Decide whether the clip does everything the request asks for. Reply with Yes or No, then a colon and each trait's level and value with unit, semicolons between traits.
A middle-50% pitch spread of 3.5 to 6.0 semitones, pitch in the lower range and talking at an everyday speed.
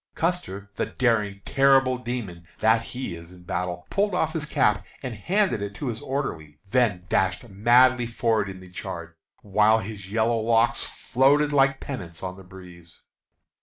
Yes: wide, 5.4 semitones; low, 110 Hz; average, 165 wpm